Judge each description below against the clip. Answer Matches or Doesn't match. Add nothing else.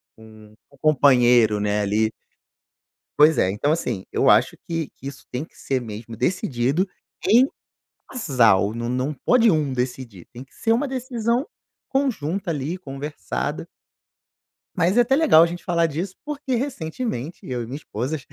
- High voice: Doesn't match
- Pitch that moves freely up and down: Matches